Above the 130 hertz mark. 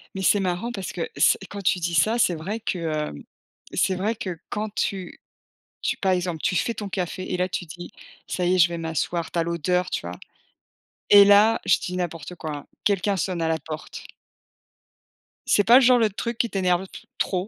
Yes: medium, 185 Hz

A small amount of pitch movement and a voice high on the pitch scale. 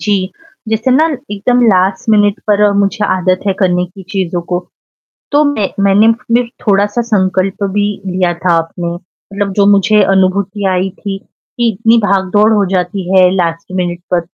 Yes: narrow, 2.2 semitones; high, 195 Hz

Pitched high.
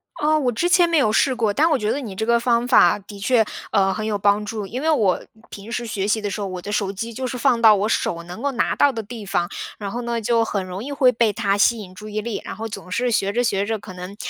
Yes: high, 220 Hz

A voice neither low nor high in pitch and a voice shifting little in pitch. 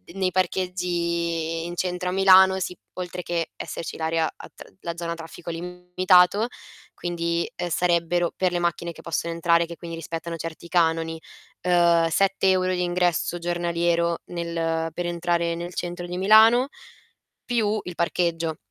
Yes: medium, 175 Hz; narrow, 1.2 semitones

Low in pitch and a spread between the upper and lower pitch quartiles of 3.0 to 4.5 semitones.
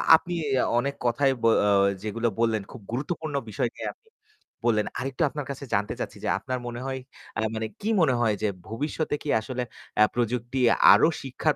Yes: low, 125 Hz; average, 3.7 semitones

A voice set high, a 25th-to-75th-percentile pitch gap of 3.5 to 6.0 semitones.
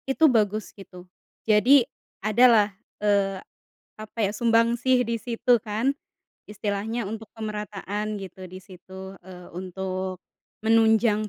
No: high, 210 Hz; average, 2.9 semitones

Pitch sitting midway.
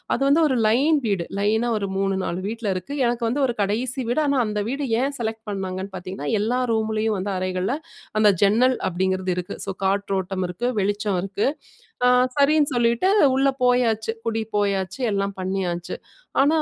No: high, 215 Hz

